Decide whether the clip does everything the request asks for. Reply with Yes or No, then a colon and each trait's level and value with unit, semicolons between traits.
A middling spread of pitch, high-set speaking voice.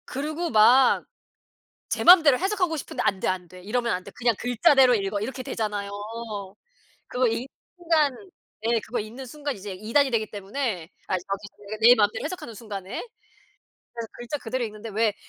Yes: average, 4.5 semitones; high, 230 Hz